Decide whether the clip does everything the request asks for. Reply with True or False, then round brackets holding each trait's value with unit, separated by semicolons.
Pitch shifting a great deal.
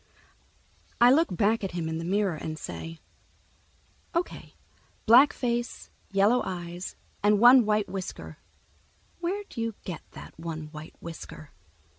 True (6.1 semitones)